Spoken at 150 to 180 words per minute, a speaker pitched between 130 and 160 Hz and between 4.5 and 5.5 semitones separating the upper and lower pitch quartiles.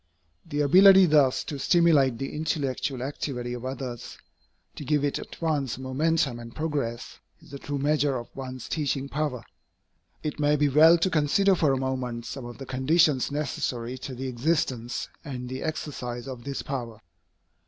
No: average, 165 wpm; low, 135 Hz; average, 3.0 semitones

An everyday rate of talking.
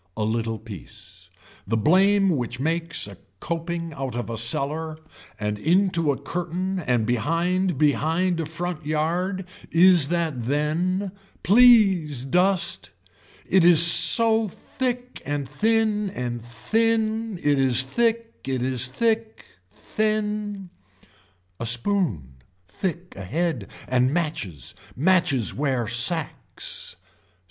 No: slow, 110 wpm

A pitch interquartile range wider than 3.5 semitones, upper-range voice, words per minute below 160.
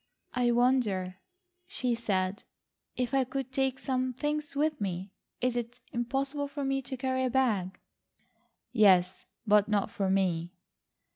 Yes: average, 5.1 semitones; high, 245 Hz; average, 140 wpm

